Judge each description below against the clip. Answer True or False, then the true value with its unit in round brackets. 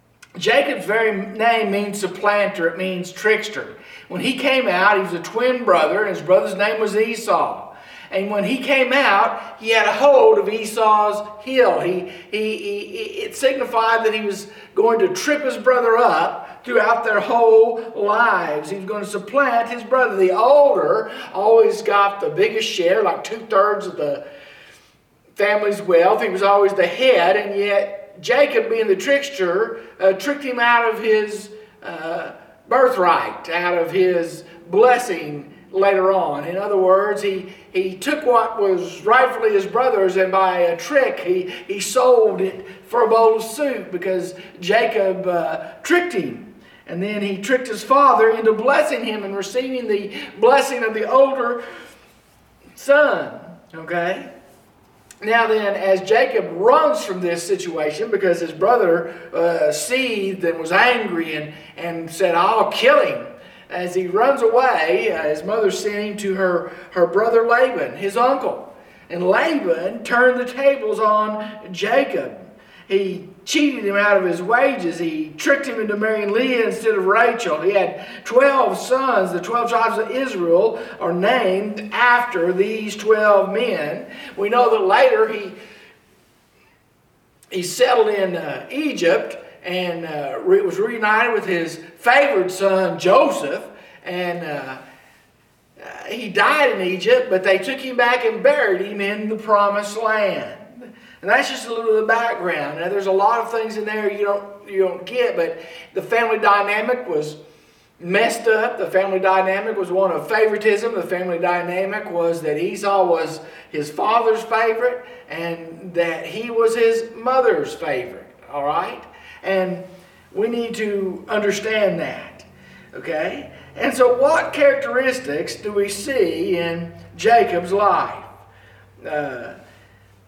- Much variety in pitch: False (4.6 semitones)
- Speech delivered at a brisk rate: False (150 wpm)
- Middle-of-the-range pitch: False (210 Hz)